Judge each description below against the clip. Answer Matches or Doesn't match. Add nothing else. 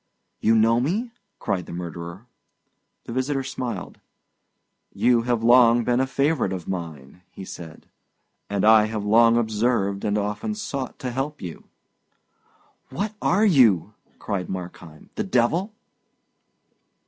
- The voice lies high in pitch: Doesn't match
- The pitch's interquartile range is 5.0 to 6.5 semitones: Matches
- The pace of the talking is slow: Matches